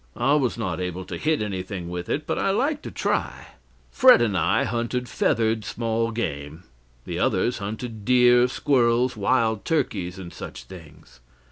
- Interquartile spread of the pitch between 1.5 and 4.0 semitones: No, average, 5.0 semitones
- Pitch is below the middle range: Yes, low, 115 Hz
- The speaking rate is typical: Yes, average, 160 wpm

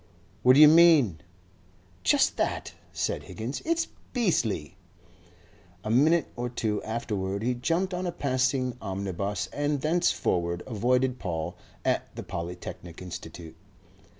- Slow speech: Yes, slow, 125 wpm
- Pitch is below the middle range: Yes, low, 120 Hz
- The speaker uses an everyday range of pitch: No, wide, 7.6 semitones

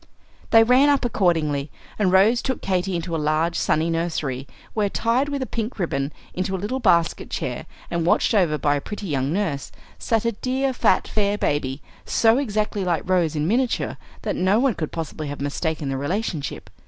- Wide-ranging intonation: Yes, wide, 6.4 semitones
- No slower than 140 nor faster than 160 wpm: No, average, 185 wpm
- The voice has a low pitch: No, medium, 185 Hz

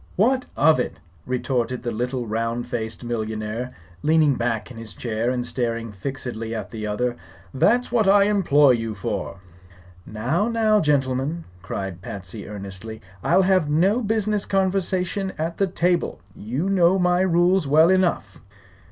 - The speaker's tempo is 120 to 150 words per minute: Yes, average, 145 wpm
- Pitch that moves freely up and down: Yes, wide, 8.4 semitones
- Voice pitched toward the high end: No, low, 135 Hz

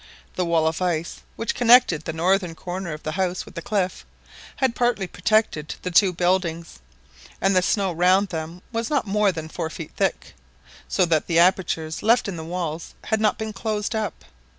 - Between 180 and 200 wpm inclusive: Yes, average, 190 wpm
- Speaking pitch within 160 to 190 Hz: Yes, medium, 185 Hz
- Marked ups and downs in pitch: No, average, 4.1 semitones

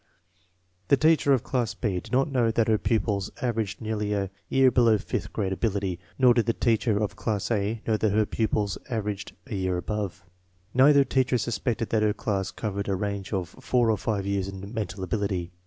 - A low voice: Yes, low, 105 Hz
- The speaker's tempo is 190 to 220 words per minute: Yes, average, 195 wpm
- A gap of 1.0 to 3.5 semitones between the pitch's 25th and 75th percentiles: Yes, average, 3.0 semitones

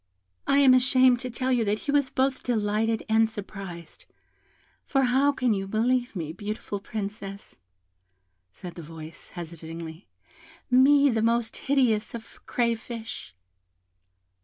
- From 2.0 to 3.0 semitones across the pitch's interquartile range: No, average, 4.5 semitones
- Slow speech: Yes, slow, 130 wpm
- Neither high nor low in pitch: No, high, 225 Hz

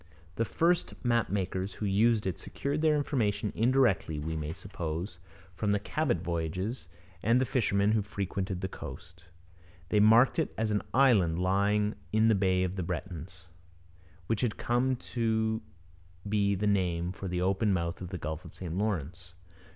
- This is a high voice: No, low, 100 Hz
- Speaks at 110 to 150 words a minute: No, average, 165 wpm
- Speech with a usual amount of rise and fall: Yes, average, 3.8 semitones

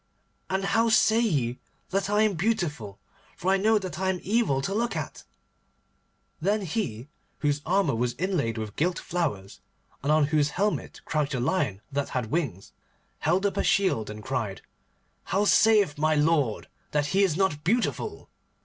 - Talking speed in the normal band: Yes, average, 165 wpm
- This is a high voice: No, medium, 160 Hz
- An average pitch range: No, wide, 6.4 semitones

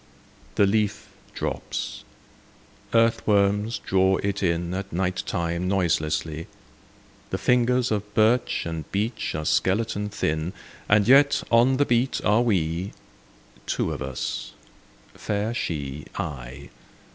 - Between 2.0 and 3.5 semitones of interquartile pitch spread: No, average, 4.9 semitones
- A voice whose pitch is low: Yes, low, 100 Hz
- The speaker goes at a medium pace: No, slow, 115 wpm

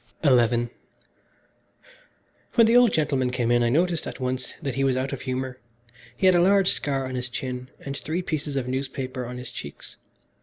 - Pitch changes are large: No, average, 3.3 semitones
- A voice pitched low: Yes, low, 130 Hz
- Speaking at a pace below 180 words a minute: No, average, 190 wpm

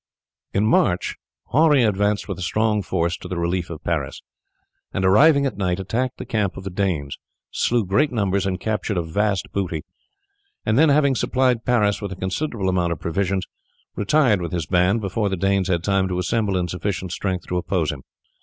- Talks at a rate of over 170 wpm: Yes, average, 190 wpm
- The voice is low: Yes, very low, 95 Hz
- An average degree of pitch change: Yes, average, 3.3 semitones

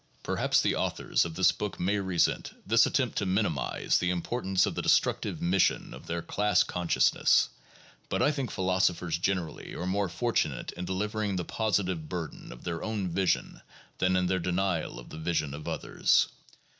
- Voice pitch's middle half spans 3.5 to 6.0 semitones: No, average, 2.8 semitones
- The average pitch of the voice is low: Yes, very low, 95 Hz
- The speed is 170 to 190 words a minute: Yes, average, 175 wpm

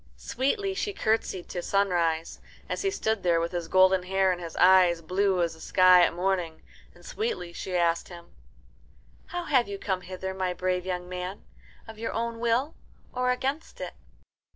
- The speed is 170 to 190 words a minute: Yes, average, 175 wpm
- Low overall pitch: No, medium, 185 Hz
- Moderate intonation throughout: Yes, average, 4.3 semitones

